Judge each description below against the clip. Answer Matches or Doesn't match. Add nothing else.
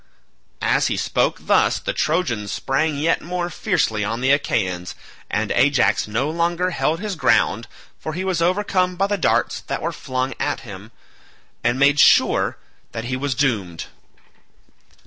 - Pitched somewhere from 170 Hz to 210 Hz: Doesn't match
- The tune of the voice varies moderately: Doesn't match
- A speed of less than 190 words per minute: Matches